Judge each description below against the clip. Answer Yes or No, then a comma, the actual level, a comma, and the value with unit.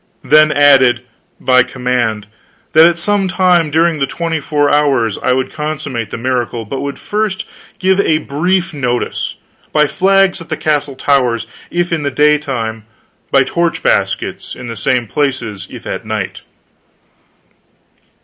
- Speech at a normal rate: Yes, average, 150 wpm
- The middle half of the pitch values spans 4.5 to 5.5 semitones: Yes, average, 4.9 semitones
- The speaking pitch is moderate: Yes, medium, 145 Hz